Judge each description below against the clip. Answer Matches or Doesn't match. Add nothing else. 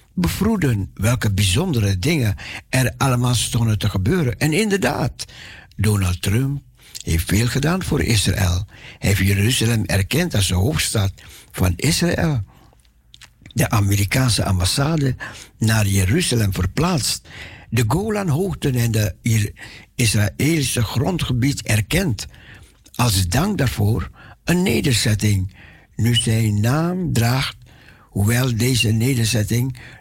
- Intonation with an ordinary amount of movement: Matches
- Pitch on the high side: Doesn't match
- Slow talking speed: Matches